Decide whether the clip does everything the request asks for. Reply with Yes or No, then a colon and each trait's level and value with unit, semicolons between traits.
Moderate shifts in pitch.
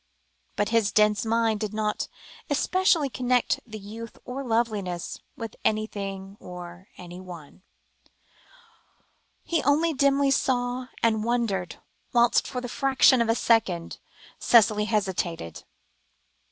Yes: average, 3.9 semitones